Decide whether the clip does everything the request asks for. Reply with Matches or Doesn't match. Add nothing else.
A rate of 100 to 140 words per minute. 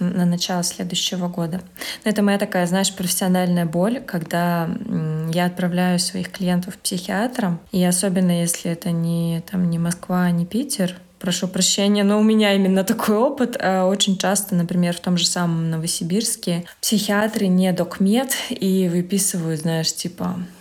Doesn't match